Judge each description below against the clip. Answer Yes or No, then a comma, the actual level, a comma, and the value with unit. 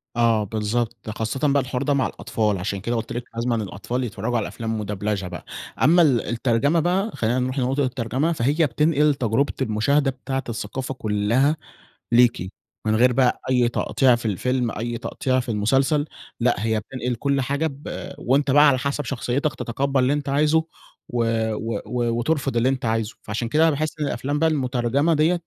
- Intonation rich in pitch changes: No, average, 3.7 semitones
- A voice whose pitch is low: Yes, low, 125 Hz